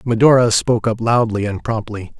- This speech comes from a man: Yes, male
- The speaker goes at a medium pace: Yes, average, 165 wpm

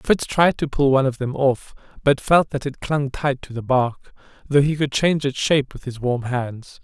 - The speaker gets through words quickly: Yes, fast, 235 wpm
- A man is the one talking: Yes, male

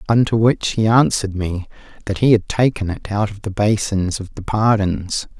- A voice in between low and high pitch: No, low, 105 Hz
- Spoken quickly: No, average, 190 wpm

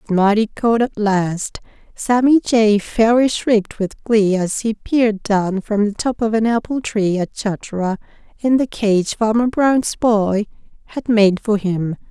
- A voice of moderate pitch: No, high, 215 Hz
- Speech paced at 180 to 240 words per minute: No, average, 165 wpm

